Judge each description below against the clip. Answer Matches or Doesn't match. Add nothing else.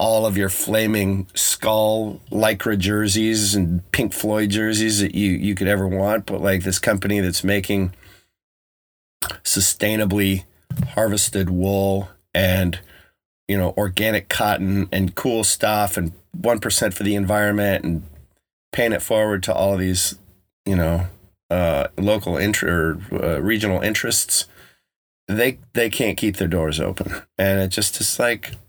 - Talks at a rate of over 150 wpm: Doesn't match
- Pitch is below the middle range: Matches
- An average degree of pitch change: Doesn't match